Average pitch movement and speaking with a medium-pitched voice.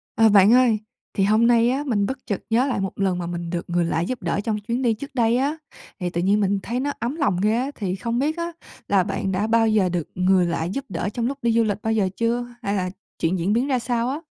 No: average, 4.4 semitones; high, 220 Hz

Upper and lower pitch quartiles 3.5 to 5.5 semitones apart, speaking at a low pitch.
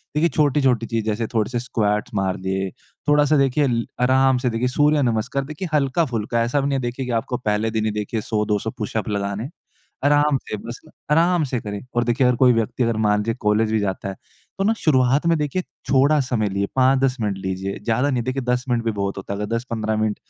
Yes: average, 4.1 semitones; low, 120 Hz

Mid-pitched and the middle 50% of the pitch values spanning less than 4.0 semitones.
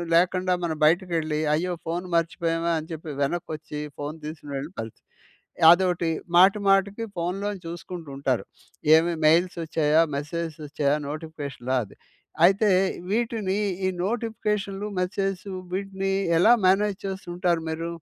Yes: medium, 175 Hz; average, 3.6 semitones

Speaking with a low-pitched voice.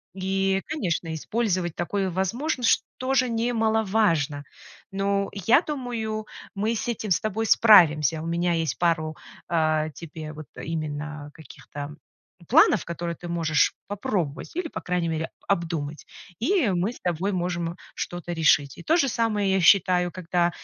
No: medium, 180 Hz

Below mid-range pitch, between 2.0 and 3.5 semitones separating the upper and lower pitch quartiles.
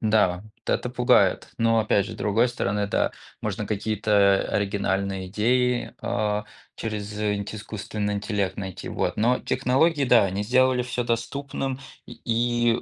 Yes: low, 110 Hz; average, 3.1 semitones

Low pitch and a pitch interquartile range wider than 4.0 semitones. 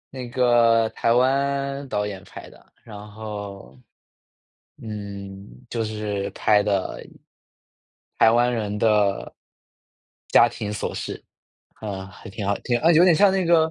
No: low, 110 Hz; average, 3.7 semitones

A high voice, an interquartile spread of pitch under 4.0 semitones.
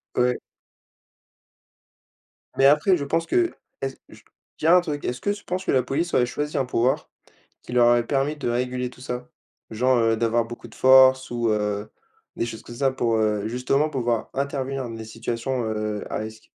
No: low, 125 Hz; average, 2.9 semitones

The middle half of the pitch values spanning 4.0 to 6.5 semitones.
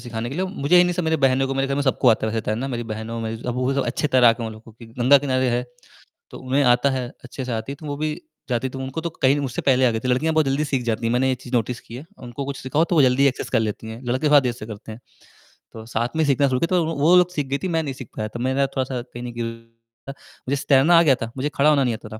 No: average, 3.0 semitones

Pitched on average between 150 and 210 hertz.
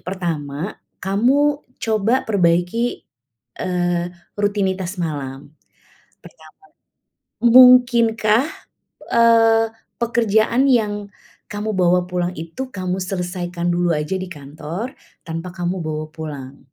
Yes: medium, 185 Hz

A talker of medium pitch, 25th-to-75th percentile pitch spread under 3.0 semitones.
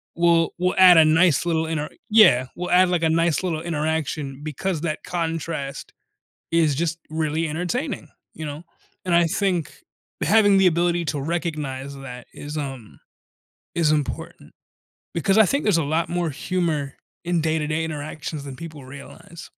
Yes: medium, 160 Hz; narrow, 2.6 semitones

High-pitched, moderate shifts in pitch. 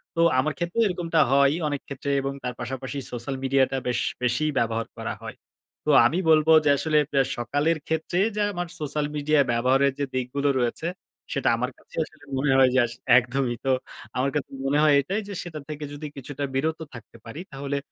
No: medium, 140 Hz; average, 3.1 semitones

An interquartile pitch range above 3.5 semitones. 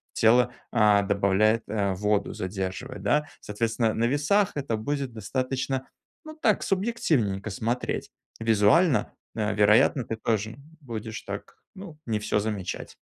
Yes: average, 4.3 semitones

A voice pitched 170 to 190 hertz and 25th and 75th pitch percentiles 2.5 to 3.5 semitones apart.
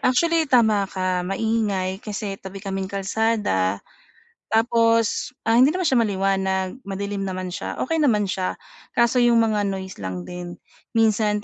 No: high, 205 Hz; average, 3.2 semitones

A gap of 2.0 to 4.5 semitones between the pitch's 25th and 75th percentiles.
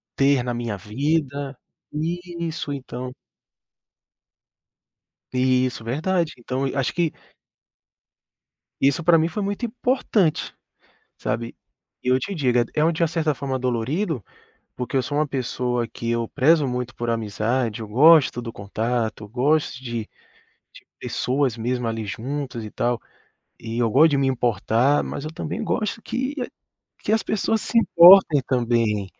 No: average, 5.0 semitones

